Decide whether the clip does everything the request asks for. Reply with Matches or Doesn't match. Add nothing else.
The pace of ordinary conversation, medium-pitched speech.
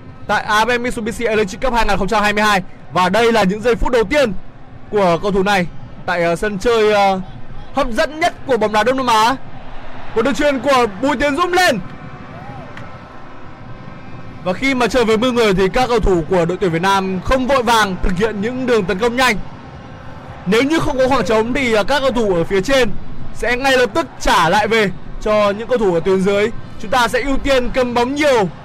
Doesn't match